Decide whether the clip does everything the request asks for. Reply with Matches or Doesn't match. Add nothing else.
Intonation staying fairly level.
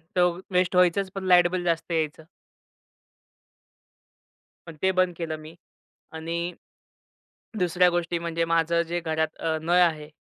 Matches